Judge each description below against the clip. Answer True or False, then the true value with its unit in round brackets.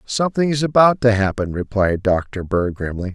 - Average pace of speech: True (170 wpm)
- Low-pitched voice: True (110 Hz)